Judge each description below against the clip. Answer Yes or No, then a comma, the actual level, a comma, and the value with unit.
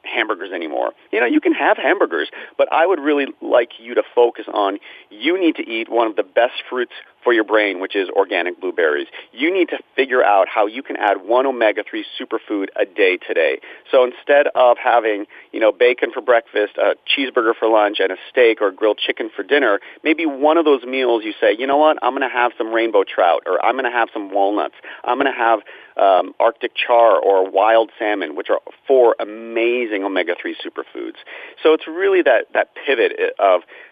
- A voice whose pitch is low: No, very high, 325 Hz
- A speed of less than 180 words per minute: No, fast, 205 wpm